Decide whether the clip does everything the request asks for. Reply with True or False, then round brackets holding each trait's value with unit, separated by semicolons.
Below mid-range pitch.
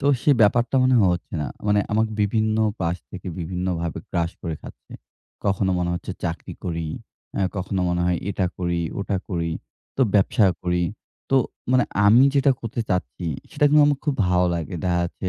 True (95 Hz)